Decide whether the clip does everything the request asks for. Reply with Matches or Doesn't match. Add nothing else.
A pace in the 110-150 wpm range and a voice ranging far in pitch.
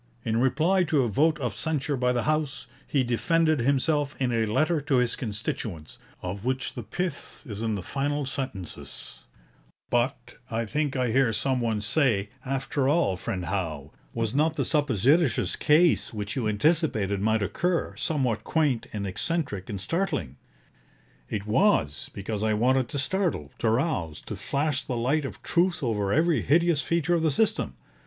Doesn't match